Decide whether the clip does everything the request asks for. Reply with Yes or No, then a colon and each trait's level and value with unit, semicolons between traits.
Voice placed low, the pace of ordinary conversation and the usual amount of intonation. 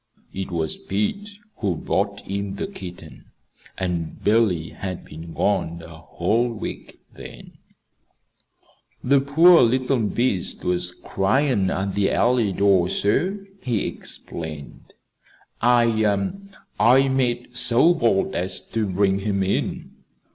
No: low, 100 Hz; slow, 120 wpm; average, 4.8 semitones